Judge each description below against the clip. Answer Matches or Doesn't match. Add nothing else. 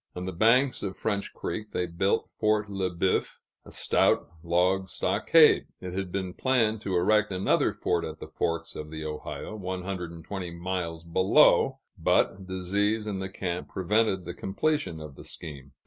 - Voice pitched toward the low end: Matches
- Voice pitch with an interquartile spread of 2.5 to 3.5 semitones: Matches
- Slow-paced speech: Doesn't match